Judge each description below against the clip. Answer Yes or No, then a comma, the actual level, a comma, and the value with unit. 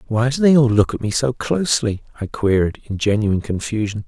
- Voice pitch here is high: No, low, 115 Hz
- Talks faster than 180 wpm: Yes, fast, 205 wpm